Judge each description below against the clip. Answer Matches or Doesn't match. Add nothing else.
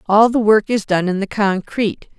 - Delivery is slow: Doesn't match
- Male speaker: Doesn't match